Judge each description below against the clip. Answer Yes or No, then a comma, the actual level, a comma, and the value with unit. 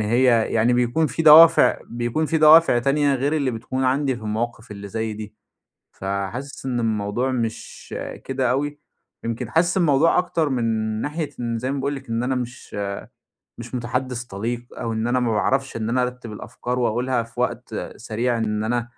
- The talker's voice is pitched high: No, low, 125 Hz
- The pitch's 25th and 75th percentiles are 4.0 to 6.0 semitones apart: No, average, 2.9 semitones